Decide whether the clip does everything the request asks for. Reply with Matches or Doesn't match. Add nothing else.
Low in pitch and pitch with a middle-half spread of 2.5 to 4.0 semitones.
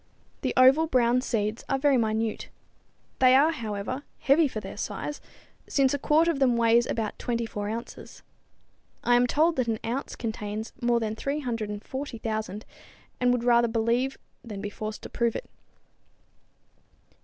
Doesn't match